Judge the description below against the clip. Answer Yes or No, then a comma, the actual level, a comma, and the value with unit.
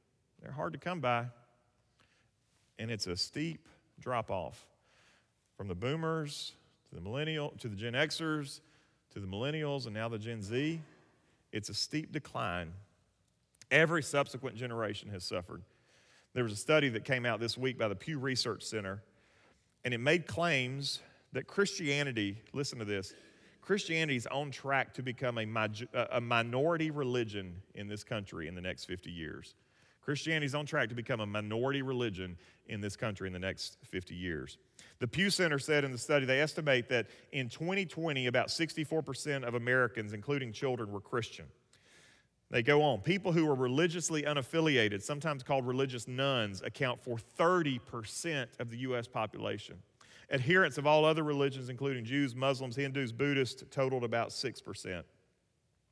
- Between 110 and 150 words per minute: No, average, 160 wpm